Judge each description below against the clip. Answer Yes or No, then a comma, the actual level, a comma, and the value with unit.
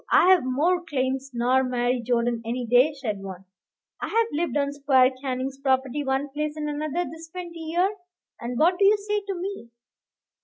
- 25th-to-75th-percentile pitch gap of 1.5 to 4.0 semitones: No, average, 4.7 semitones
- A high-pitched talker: Yes, very high, 280 Hz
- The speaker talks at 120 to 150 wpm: No, average, 175 wpm